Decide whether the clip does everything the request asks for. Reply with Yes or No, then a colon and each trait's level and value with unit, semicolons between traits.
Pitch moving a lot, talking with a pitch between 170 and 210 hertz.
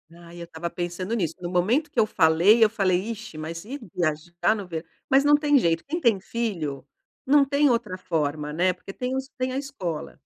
Yes: wide, 6.9 semitones; medium, 185 Hz